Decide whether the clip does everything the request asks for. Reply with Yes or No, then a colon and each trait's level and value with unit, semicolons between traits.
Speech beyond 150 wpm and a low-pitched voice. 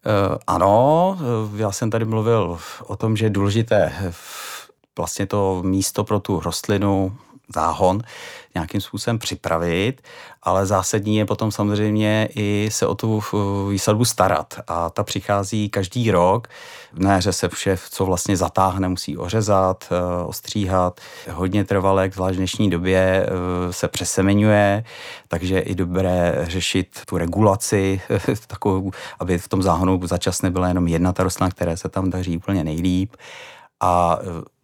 No: average, 135 wpm; very low, 95 Hz